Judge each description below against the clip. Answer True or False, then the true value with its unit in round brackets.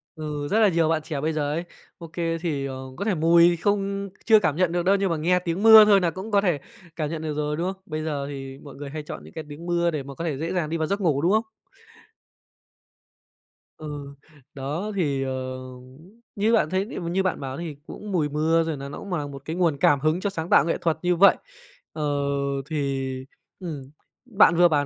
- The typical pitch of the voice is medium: True (165 Hz)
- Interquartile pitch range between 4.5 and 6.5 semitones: False (3.9 semitones)